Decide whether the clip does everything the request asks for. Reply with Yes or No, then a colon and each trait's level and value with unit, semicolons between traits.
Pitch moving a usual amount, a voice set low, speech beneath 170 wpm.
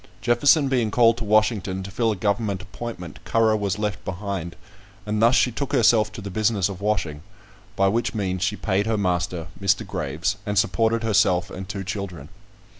No: average, 3.2 semitones; low, 105 Hz; average, 185 wpm